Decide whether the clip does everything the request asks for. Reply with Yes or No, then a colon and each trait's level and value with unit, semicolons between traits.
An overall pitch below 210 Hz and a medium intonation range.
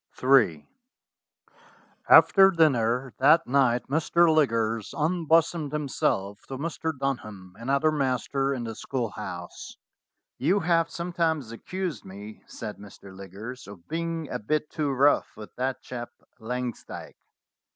No: low, 135 Hz; wide, 6.0 semitones